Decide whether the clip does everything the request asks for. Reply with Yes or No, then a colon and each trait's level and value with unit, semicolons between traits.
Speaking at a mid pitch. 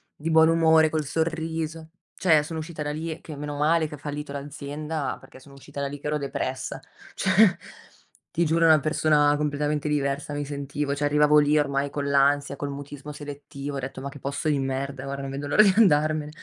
Yes: medium, 145 Hz